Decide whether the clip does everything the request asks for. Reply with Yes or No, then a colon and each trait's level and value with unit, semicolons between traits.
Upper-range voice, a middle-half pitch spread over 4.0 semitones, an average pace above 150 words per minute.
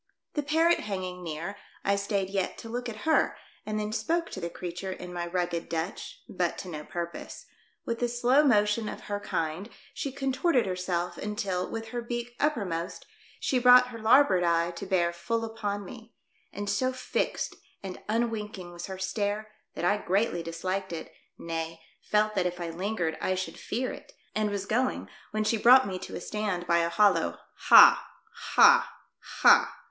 Yes: high, 200 Hz; average, 4.6 semitones; average, 180 wpm